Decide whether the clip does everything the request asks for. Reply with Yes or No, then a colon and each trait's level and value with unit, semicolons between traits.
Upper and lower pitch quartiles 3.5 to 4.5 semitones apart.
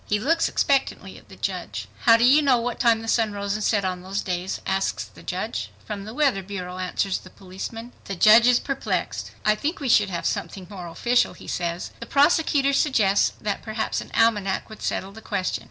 Yes: average, 4.2 semitones